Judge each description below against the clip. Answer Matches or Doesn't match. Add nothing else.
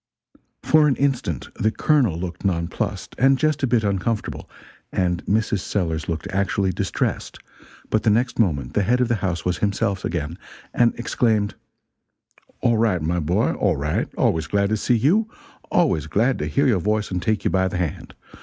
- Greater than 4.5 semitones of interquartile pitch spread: Matches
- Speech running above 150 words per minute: Matches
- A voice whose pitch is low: Matches